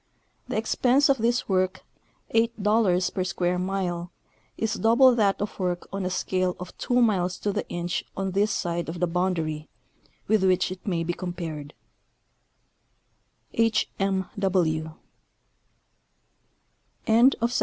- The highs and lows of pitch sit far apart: No, average, 3.4 semitones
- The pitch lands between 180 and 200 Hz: Yes, medium, 185 Hz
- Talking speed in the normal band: No, slow, 130 wpm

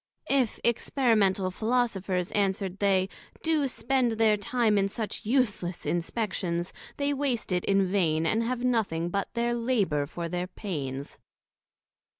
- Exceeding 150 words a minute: No, slow, 135 wpm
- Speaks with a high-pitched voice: Yes, high, 205 Hz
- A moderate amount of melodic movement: Yes, average, 4.7 semitones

